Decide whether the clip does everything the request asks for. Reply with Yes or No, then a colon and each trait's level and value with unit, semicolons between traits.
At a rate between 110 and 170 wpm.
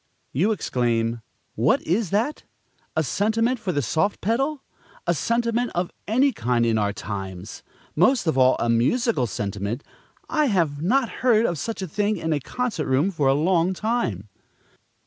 Yes: average, 165 wpm